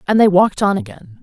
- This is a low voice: No, high, 190 Hz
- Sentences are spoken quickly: Yes, fast, 245 wpm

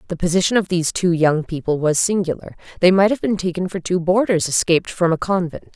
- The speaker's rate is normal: No, fast, 220 wpm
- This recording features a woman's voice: Yes, female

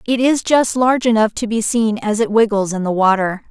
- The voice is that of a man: No, female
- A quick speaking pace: Yes, fast, 240 wpm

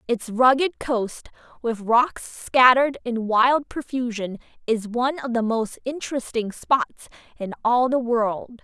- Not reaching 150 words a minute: Yes, average, 140 wpm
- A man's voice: No, female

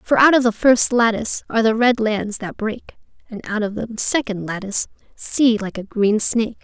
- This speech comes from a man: No, female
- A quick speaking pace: Yes, fast, 210 wpm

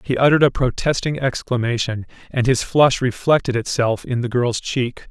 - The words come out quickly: No, average, 165 wpm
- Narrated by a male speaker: Yes, male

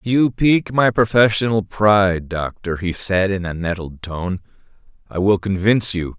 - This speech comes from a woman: No, male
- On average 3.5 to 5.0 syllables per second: Yes, 4.6 syllables/s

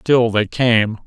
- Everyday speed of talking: Yes, average, 170 wpm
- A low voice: Yes, low, 115 Hz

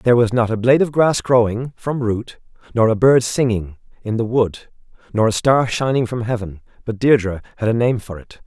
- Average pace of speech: No, fast, 215 wpm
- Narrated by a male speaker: Yes, male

